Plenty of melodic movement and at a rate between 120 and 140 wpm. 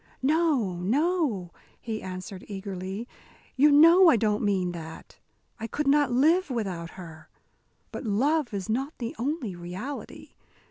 Yes: wide, 7.5 semitones; slow, 135 wpm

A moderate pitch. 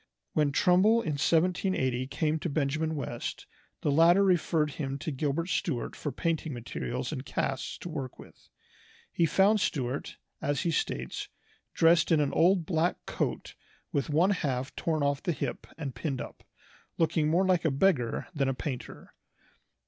Yes: medium, 155 Hz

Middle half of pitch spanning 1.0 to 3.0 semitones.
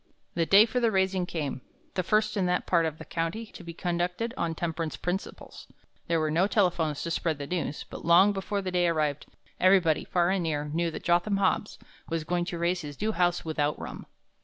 Yes: average, 2.7 semitones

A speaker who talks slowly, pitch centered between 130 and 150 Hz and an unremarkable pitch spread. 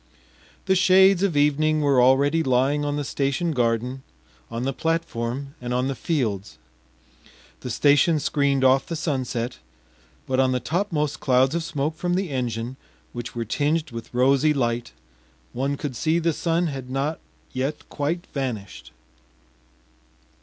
No: average, 145 wpm; medium, 140 Hz; average, 3.7 semitones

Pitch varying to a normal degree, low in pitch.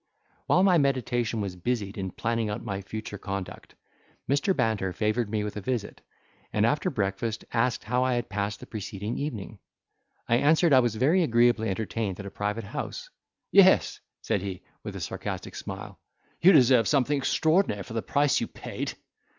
Yes: average, 4.0 semitones; low, 115 Hz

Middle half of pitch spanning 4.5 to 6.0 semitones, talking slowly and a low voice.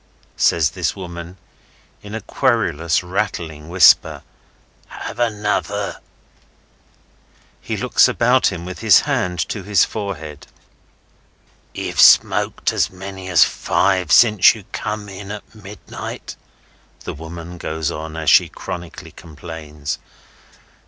No: average, 4.0 semitones; slow, 115 wpm; very low, 90 Hz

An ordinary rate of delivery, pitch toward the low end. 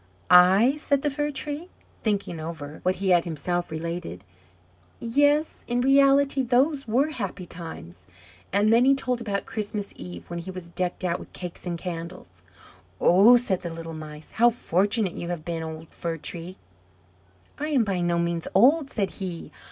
No: average, 170 wpm; medium, 185 Hz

